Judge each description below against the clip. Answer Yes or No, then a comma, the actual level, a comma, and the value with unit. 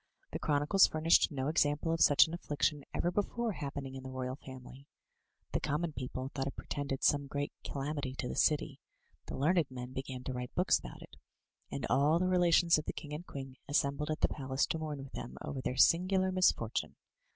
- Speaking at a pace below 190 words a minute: No, average, 200 wpm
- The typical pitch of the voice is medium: Yes, medium, 145 Hz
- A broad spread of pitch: No, average, 3.4 semitones